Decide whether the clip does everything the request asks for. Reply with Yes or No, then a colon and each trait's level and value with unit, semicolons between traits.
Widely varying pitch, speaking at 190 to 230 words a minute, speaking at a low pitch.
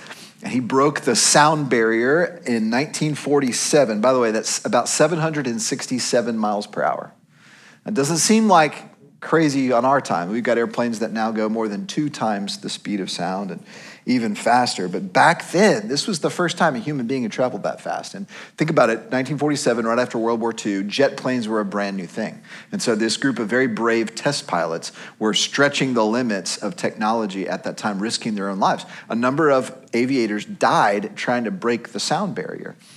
Yes: wide, 5.8 semitones; average, 195 wpm; low, 130 Hz